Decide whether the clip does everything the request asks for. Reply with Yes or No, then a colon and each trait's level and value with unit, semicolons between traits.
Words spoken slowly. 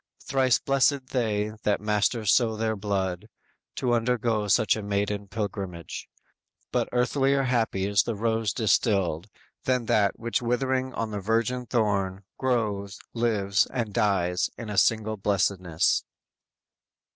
Yes: slow, 120 wpm